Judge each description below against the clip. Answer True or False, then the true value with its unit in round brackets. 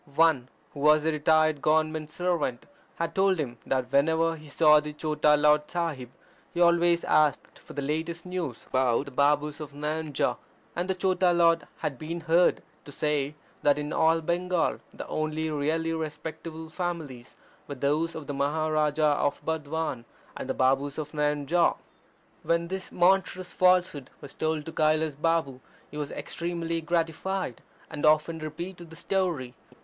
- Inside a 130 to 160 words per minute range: True (155 wpm)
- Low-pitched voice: False (155 Hz)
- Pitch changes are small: True (2.2 semitones)